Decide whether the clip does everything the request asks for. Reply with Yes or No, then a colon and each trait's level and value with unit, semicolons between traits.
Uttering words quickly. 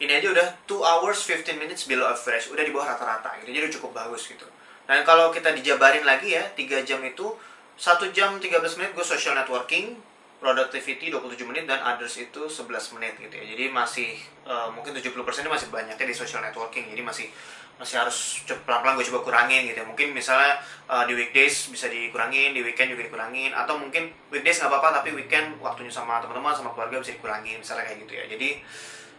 Yes: fast, 200 wpm